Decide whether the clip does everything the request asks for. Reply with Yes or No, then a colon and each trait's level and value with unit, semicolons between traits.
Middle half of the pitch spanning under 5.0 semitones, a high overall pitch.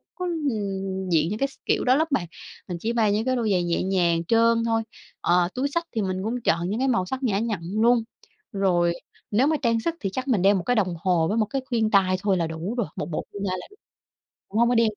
Yes: average, 4.4 semitones; high, 210 Hz